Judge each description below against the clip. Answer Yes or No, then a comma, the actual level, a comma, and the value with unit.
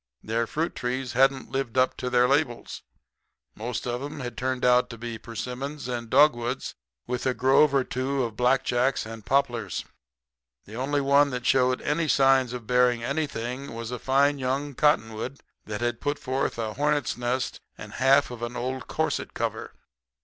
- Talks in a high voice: No, low, 125 Hz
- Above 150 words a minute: Yes, average, 170 wpm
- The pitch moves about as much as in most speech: No, narrow, 2.3 semitones